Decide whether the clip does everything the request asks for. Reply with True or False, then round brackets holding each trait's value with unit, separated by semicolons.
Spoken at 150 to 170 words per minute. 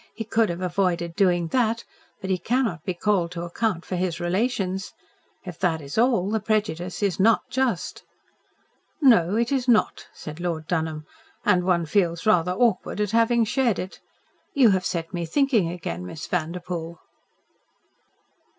True (160 wpm)